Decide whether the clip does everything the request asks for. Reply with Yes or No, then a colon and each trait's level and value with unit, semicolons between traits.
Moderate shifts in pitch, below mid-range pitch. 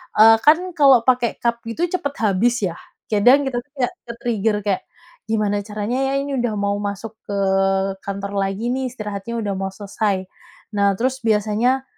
No: average, 3.6 semitones; high, 220 Hz